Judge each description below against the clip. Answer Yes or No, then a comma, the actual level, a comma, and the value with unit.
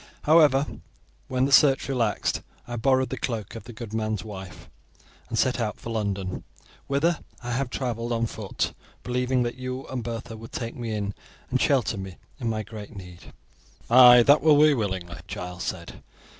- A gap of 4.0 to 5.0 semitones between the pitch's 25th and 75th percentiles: No, average, 3.5 semitones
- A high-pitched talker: No, low, 115 Hz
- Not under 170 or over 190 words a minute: Yes, average, 175 wpm